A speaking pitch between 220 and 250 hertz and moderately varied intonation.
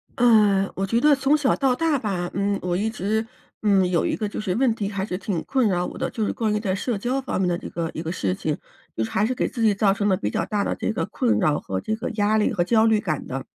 No: high, 205 Hz; average, 3.7 semitones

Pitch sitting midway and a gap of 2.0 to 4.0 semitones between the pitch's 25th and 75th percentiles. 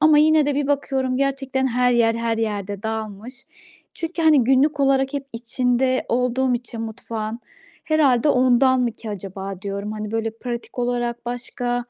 No: high, 245 Hz; average, 3.0 semitones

